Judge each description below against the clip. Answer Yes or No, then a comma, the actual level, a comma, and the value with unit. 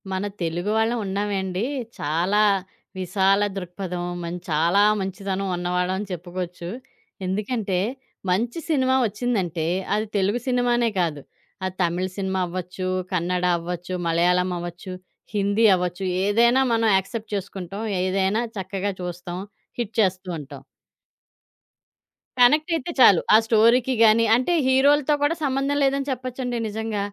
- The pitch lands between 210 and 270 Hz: No, high, 195 Hz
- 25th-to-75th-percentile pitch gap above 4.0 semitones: Yes, average, 4.4 semitones